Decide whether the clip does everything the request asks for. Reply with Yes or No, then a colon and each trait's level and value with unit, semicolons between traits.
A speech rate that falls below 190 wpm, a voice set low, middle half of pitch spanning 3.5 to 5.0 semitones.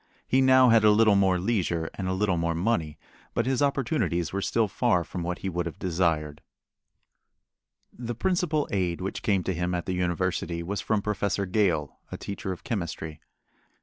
Yes: average, 180 wpm; very low, 95 Hz; average, 4.5 semitones